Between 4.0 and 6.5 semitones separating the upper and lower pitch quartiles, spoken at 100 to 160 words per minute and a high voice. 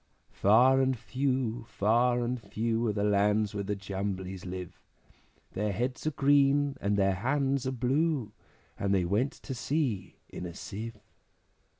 No: average, 4.8 semitones; average, 155 wpm; low, 115 Hz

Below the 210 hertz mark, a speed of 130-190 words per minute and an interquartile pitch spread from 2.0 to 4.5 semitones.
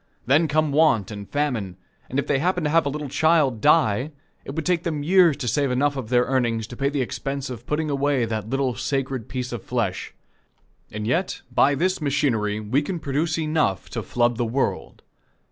No: medium, 140 Hz; average, 200 wpm; average, 3.9 semitones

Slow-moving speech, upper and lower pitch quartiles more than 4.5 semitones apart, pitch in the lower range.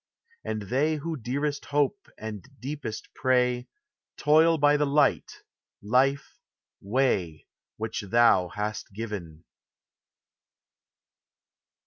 Yes: slow, 90 wpm; wide, 5.4 semitones; low, 125 Hz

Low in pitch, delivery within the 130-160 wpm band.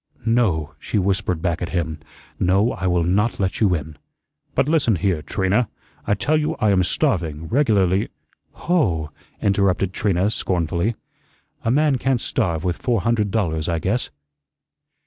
Yes: very low, 95 Hz; average, 155 wpm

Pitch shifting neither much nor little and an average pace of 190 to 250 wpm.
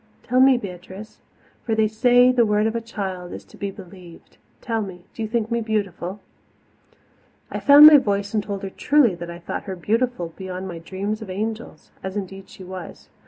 Yes: average, 3.4 semitones; fast, 205 wpm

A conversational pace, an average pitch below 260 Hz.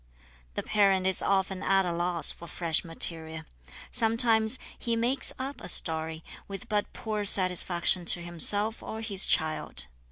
Yes: average, 150 wpm; high, 190 Hz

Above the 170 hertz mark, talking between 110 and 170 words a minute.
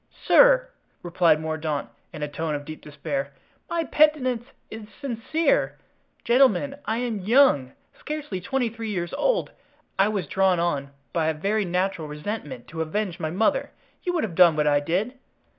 Yes: high, 190 Hz; average, 160 wpm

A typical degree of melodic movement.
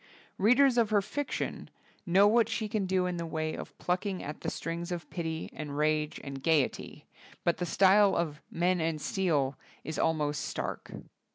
Yes: average, 4.2 semitones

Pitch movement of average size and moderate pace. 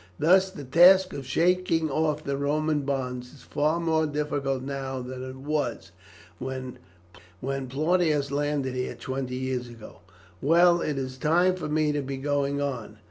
Yes: average, 3.1 semitones; average, 155 wpm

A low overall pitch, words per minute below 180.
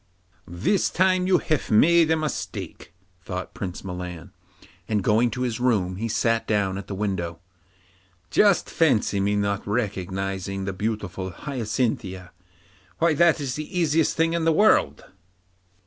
Yes: low, 105 Hz; average, 140 wpm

